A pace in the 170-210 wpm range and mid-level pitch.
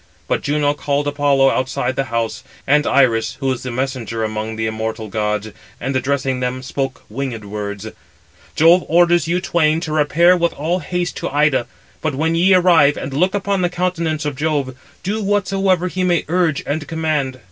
Yes: average, 180 wpm; medium, 145 Hz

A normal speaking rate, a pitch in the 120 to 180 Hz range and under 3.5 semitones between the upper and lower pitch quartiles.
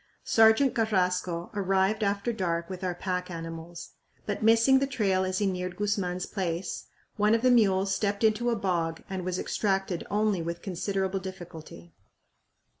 No: average, 155 wpm; high, 190 Hz; average, 2.9 semitones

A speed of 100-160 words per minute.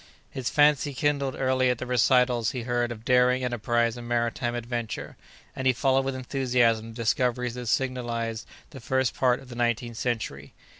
No: average, 170 wpm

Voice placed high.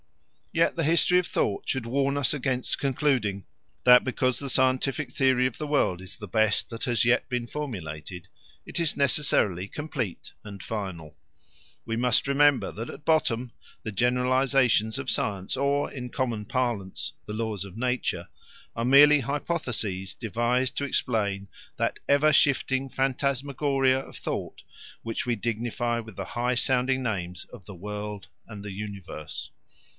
No: low, 125 Hz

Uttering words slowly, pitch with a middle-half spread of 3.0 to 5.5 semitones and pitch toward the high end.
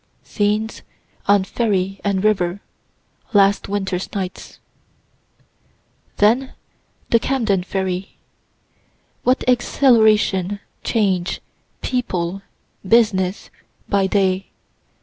No: slow, 75 wpm; narrow, 2.6 semitones; high, 200 Hz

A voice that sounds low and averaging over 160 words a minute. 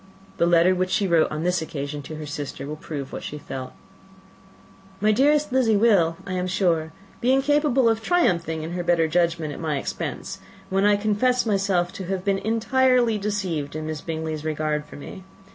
No: medium, 180 Hz; average, 190 wpm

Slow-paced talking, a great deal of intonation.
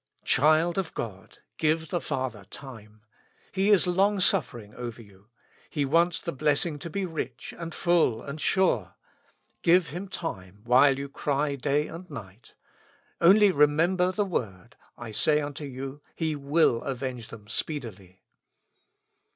No: average, 145 wpm; wide, 6.1 semitones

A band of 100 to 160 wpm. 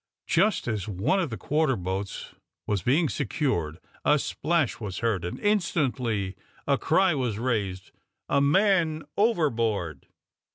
Yes: slow, 135 wpm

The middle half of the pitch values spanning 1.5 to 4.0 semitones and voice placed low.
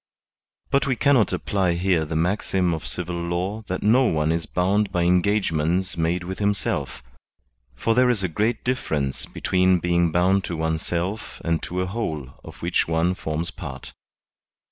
Yes: average, 3.4 semitones; very low, 90 Hz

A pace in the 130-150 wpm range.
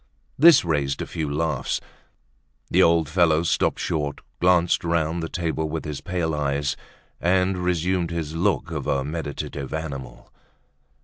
Yes: average, 140 wpm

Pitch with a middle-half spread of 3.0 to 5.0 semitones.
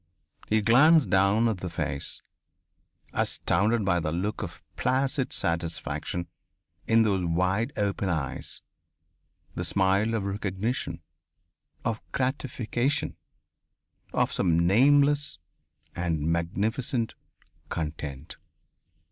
No: wide, 5.5 semitones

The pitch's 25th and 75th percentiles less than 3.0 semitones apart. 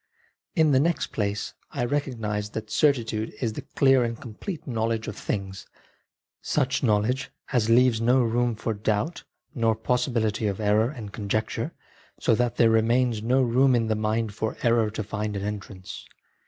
Yes: narrow, 2.6 semitones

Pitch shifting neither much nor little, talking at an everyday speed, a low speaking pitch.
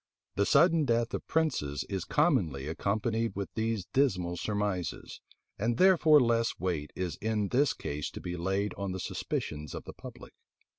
Yes: average, 5.0 semitones; average, 160 wpm; low, 100 Hz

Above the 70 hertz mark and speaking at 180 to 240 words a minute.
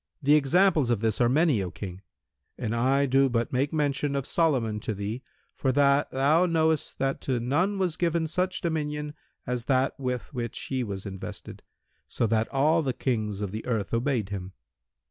Yes: low, 135 Hz; average, 185 wpm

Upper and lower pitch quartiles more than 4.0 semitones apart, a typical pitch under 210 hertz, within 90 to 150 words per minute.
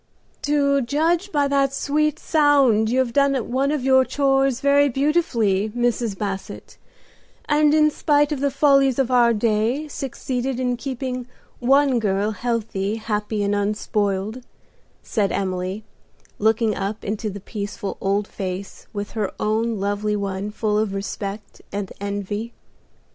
No: average, 5.0 semitones; high, 230 Hz; average, 140 wpm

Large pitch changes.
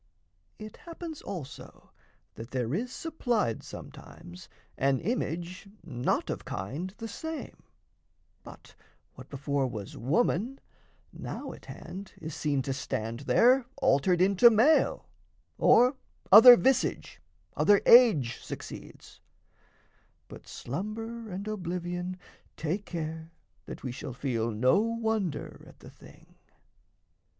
Yes: wide, 8.7 semitones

